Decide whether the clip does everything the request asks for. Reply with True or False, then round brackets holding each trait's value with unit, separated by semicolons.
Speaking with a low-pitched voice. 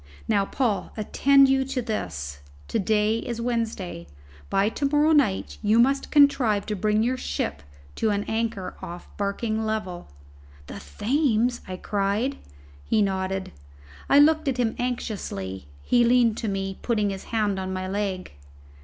False (215 Hz)